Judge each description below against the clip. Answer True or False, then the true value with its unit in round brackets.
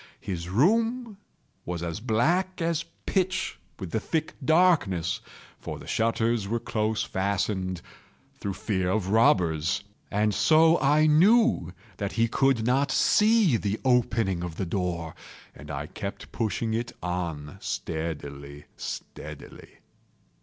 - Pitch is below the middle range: True (110 Hz)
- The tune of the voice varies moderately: False (8.9 semitones)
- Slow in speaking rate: True (125 wpm)